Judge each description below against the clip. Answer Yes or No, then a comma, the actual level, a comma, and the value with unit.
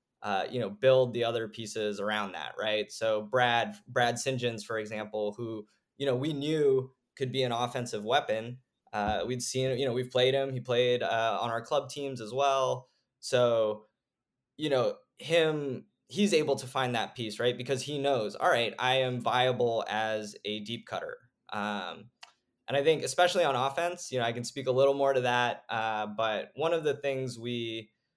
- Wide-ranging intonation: No, average, 3.2 semitones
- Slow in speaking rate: No, average, 190 wpm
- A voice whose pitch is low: Yes, low, 125 Hz